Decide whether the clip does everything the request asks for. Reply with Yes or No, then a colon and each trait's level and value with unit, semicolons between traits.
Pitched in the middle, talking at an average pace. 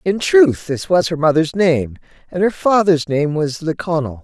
Yes: medium, 170 Hz; average, 185 wpm